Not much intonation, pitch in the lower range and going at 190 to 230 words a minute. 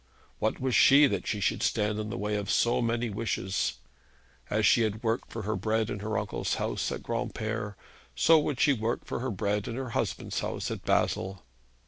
Yes: narrow, 2.3 semitones; low, 110 Hz; average, 200 wpm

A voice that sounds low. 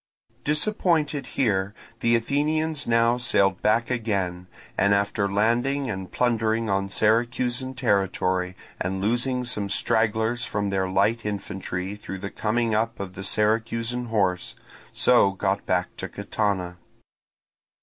Yes: low, 110 Hz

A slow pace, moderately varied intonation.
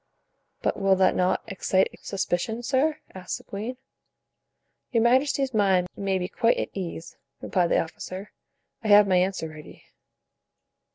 No: average, 145 wpm; average, 3.9 semitones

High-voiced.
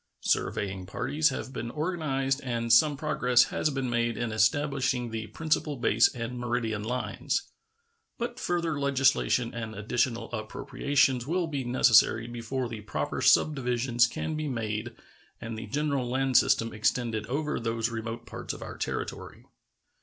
No: low, 125 Hz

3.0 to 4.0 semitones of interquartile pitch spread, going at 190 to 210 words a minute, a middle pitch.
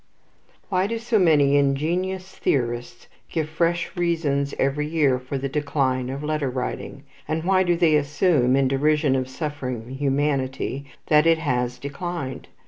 No: average, 3.7 semitones; average, 145 wpm; medium, 145 Hz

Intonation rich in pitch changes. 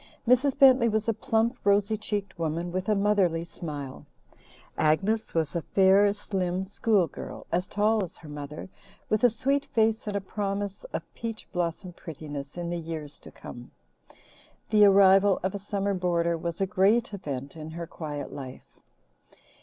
No: average, 4.2 semitones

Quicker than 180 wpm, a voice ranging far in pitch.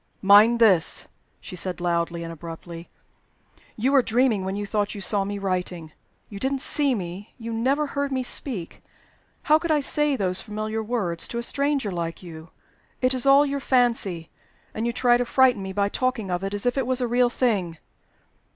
Yes: average, 190 wpm; wide, 5.7 semitones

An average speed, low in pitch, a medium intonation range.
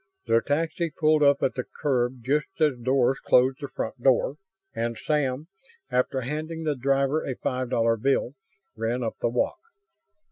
Yes: average, 165 wpm; low, 130 Hz; average, 3.3 semitones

